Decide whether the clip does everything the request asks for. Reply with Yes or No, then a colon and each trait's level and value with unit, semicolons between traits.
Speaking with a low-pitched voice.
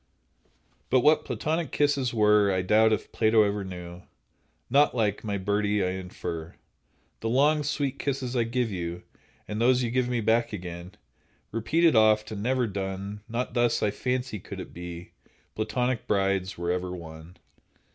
Yes: low, 110 Hz